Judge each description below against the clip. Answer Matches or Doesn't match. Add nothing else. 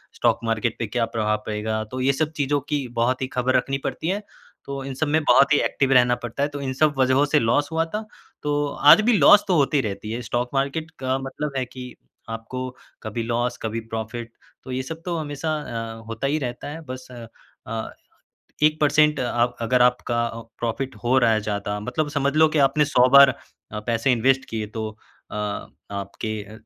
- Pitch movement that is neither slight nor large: Matches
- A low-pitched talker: Matches